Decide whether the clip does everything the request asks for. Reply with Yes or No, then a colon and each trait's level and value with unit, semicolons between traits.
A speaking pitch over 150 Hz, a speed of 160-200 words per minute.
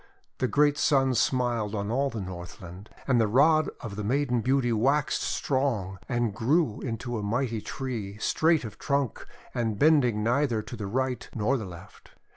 No: low, 120 Hz; average, 170 wpm